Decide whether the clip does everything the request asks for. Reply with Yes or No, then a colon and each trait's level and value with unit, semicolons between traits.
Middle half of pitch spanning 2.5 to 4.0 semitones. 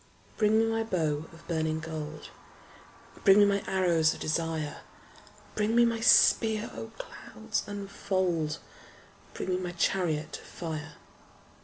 No: average, 4.8 semitones